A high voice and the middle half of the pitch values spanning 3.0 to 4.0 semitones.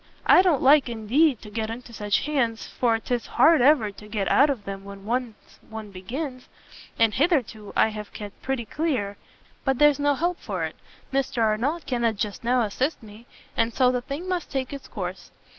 No: high, 240 Hz; average, 4.7 semitones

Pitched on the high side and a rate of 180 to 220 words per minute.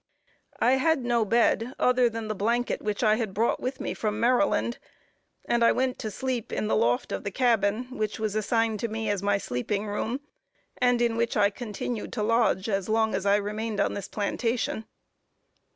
Yes: high, 220 Hz; average, 195 wpm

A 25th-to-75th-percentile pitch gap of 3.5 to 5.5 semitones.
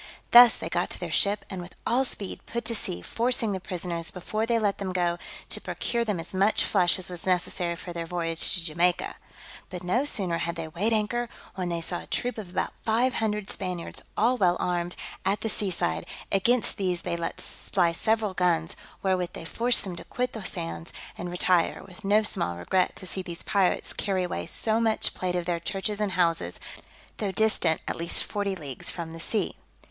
Yes: average, 3.8 semitones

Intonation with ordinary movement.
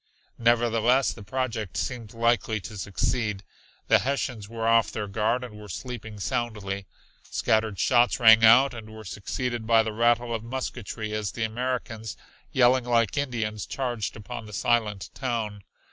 No: narrow, 2.2 semitones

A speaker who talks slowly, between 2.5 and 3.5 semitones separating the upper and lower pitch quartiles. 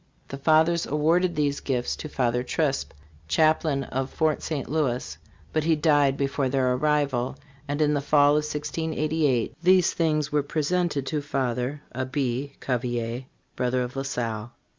No: average, 155 wpm; average, 3.2 semitones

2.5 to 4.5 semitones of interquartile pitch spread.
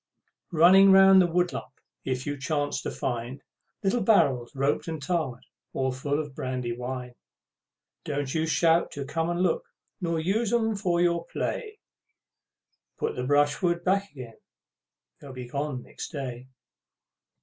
No: average, 5.2 semitones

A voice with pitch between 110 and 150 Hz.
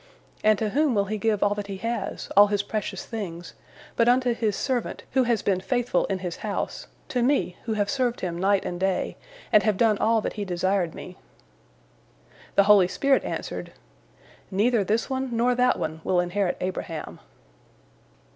No: high, 205 Hz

